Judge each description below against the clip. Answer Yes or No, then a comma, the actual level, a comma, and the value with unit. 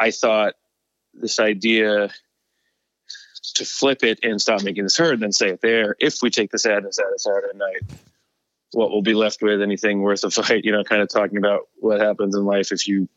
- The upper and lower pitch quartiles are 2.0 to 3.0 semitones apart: No, average, 5.2 semitones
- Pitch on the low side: Yes, low, 105 Hz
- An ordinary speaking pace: No, fast, 215 wpm